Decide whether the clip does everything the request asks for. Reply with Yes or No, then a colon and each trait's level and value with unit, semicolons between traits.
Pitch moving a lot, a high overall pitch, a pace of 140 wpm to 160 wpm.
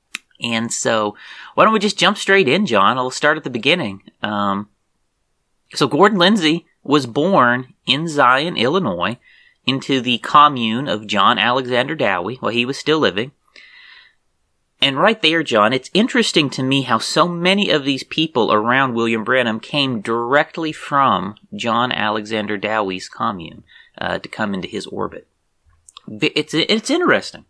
No: wide, 6.2 semitones; low, 135 Hz; average, 155 wpm